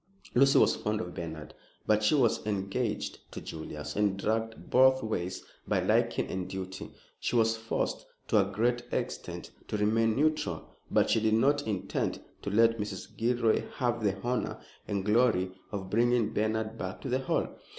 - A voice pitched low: Yes, low, 110 Hz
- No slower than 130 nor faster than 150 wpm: No, average, 170 wpm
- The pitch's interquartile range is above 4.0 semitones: No, average, 3.5 semitones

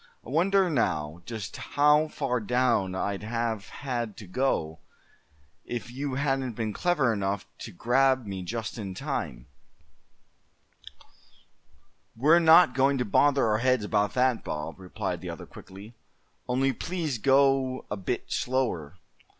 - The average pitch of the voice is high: No, low, 120 Hz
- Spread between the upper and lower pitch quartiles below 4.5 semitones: No, average, 5.0 semitones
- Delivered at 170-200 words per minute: No, slow, 135 wpm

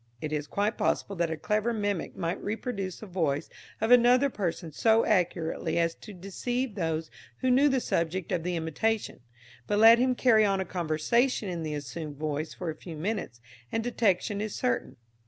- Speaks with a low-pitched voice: No, high, 190 Hz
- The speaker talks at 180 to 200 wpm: Yes, average, 185 wpm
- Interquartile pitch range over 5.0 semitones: Yes, wide, 5.5 semitones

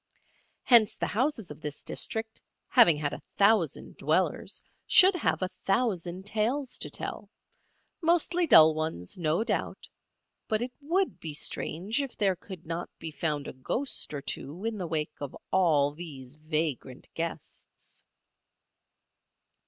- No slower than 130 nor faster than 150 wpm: Yes, average, 140 wpm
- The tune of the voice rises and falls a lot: Yes, wide, 6.7 semitones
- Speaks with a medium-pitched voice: Yes, medium, 180 Hz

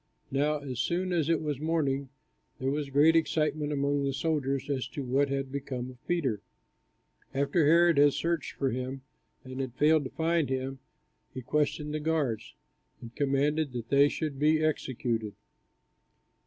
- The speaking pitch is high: No, medium, 140 Hz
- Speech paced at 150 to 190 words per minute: Yes, average, 160 wpm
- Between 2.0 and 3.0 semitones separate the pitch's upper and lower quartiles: Yes, narrow, 2.6 semitones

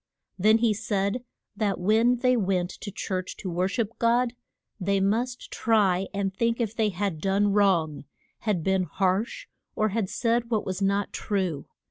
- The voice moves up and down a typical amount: Yes, average, 3.2 semitones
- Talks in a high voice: Yes, high, 200 Hz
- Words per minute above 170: No, average, 165 wpm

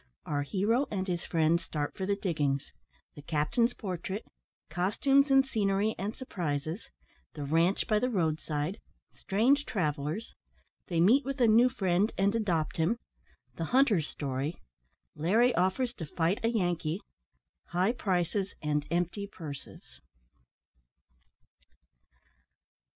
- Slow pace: Yes, slow, 125 wpm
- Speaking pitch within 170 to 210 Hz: Yes, medium, 185 Hz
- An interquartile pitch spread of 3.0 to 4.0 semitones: No, wide, 5.6 semitones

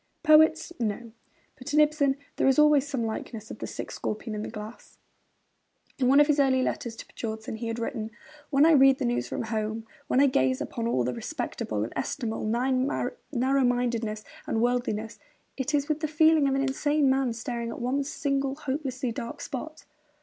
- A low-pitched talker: No, very high, 255 Hz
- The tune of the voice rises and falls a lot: No, average, 3.8 semitones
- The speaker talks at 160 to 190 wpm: Yes, average, 185 wpm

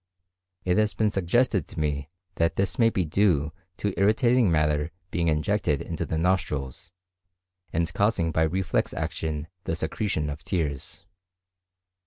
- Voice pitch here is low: Yes, very low, 85 Hz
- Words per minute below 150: Yes, average, 140 wpm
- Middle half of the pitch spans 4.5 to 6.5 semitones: Yes, average, 4.8 semitones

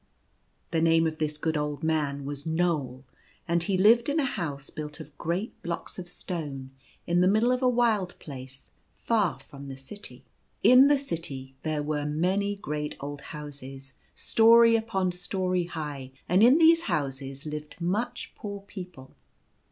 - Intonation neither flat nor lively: No, wide, 5.7 semitones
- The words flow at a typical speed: Yes, average, 160 wpm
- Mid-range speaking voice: Yes, medium, 165 Hz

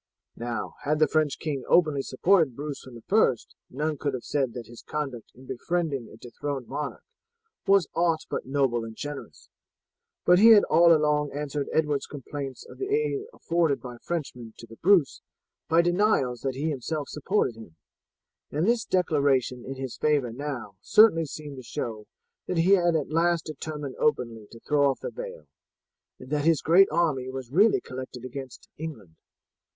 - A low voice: No, medium, 145 Hz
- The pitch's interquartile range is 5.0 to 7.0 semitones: No, average, 4.4 semitones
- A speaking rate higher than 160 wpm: Yes, average, 175 wpm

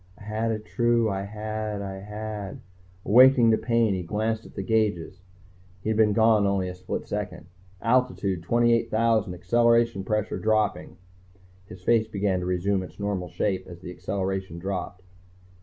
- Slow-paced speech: No, average, 160 wpm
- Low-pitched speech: Yes, low, 105 Hz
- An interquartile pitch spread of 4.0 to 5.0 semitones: No, average, 2.8 semitones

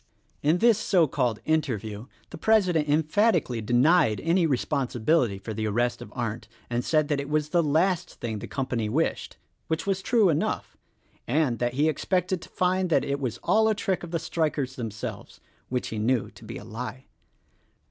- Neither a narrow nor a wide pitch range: No, wide, 6.2 semitones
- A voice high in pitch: No, medium, 145 Hz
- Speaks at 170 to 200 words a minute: Yes, average, 190 wpm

